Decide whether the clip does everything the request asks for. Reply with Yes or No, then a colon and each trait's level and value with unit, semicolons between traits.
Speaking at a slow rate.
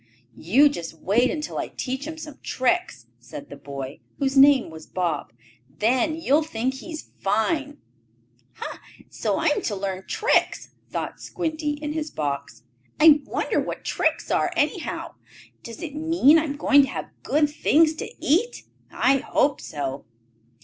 No: average, 155 wpm